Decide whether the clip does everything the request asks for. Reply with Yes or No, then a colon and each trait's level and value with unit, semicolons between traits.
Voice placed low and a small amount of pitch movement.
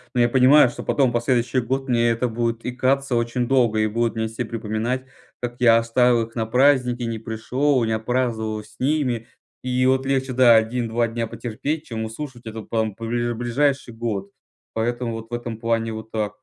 Yes: low, 120 Hz; narrow, 2.1 semitones